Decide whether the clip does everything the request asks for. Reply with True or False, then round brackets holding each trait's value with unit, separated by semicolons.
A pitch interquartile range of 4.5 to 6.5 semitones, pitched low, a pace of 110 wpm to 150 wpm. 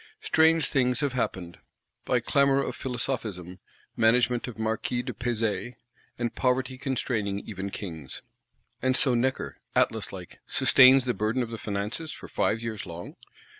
False (3.6 semitones; 120 Hz; 145 wpm)